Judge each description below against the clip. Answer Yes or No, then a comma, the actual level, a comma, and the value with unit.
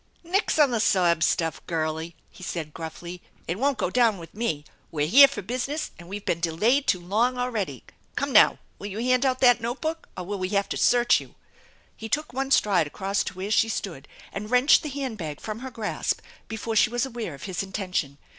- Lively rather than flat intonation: Yes, wide, 6.2 semitones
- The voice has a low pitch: No, high, 210 Hz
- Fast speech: Yes, fast, 225 wpm